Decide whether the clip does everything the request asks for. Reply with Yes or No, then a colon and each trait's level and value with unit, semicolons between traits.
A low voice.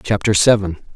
Yes: low, 100 Hz